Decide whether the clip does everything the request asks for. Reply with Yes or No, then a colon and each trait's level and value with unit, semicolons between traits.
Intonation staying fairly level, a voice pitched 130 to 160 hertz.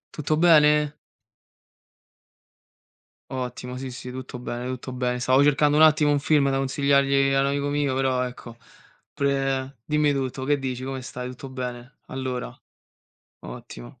Yes: narrow, 2.1 semitones; low, 135 Hz